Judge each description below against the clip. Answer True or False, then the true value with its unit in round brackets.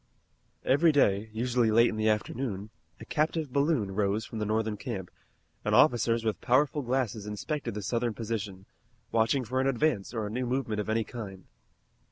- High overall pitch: False (115 Hz)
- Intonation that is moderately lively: True (3.4 semitones)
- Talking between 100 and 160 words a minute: False (175 wpm)